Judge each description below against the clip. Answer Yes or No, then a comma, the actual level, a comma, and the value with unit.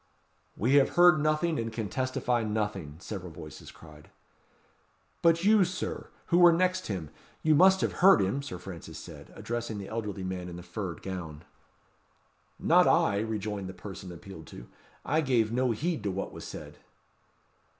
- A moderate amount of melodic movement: No, wide, 8.4 semitones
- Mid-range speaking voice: No, low, 110 Hz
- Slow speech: No, average, 165 wpm